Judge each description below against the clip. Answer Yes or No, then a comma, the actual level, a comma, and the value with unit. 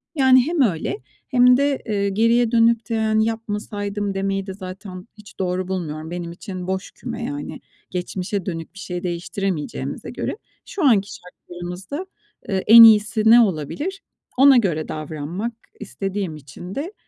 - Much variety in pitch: No, average, 4.2 semitones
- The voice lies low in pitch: No, high, 195 Hz